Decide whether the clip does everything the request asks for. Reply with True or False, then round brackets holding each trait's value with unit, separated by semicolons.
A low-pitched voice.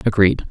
True (105 Hz)